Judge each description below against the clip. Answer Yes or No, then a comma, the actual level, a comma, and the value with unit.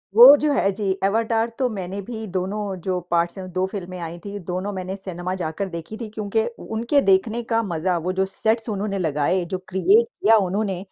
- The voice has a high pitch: Yes, high, 195 Hz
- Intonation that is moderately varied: Yes, average, 3.1 semitones